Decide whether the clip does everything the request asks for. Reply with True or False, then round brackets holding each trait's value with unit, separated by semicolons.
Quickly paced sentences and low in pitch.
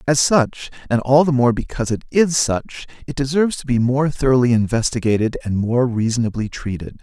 False (180 wpm; 125 Hz)